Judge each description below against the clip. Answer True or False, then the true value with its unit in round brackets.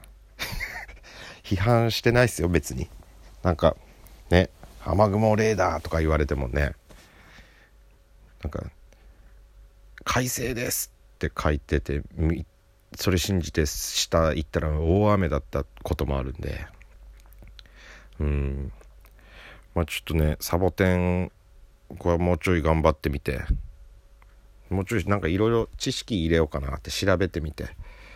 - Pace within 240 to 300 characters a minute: True (255 characters per minute)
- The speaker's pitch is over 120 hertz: False (85 Hz)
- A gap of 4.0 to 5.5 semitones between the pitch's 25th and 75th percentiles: False (3.6 semitones)